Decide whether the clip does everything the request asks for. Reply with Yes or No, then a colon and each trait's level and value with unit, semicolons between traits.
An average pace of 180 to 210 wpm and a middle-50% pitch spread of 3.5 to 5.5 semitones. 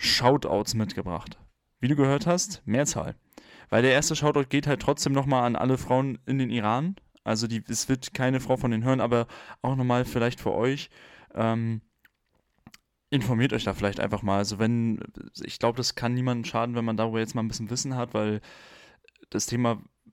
No: fast, 190 wpm; average, 2.7 semitones